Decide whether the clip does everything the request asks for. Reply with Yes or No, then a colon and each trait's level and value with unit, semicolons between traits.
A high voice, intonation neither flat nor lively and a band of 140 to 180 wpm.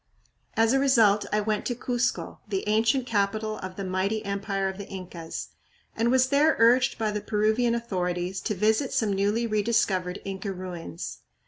Yes: high, 210 Hz; average, 3.1 semitones; average, 175 wpm